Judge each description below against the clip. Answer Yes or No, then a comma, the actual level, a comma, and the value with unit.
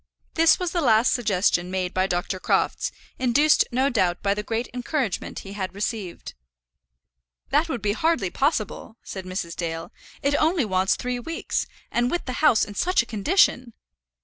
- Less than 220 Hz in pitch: No, high, 225 Hz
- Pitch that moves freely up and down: Yes, wide, 6.7 semitones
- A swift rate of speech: No, average, 170 wpm